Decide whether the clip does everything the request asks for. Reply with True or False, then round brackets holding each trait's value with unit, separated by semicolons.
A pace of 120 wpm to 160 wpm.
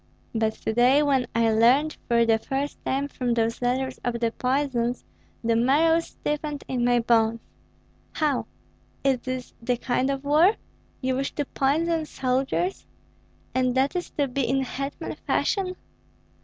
True (155 wpm)